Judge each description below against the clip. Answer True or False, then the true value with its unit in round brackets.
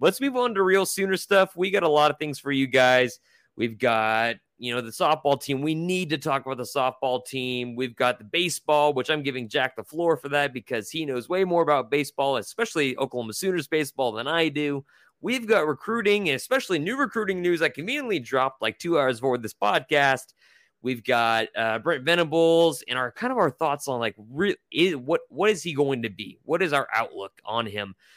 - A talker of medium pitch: True (145 Hz)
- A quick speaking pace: True (215 wpm)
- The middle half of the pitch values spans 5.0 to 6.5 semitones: True (5.3 semitones)